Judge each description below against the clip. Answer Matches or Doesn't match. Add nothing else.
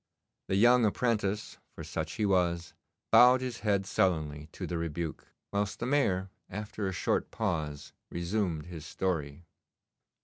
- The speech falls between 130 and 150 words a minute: Matches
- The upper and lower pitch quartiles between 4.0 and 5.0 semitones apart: Matches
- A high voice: Doesn't match